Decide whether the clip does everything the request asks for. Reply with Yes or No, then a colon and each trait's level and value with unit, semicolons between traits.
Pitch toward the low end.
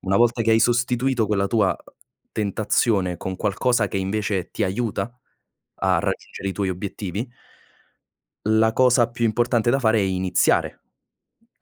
Yes: low, 110 Hz